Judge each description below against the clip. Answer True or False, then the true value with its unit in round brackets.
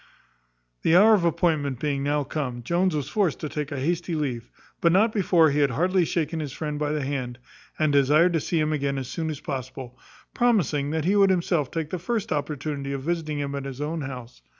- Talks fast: True (220 wpm)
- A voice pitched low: False (150 Hz)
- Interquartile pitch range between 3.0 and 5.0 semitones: True (3.4 semitones)